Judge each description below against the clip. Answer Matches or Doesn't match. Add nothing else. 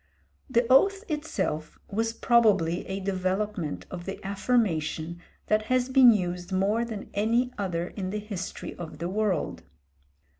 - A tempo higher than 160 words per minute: Doesn't match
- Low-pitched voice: Doesn't match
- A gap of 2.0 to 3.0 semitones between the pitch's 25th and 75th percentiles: Doesn't match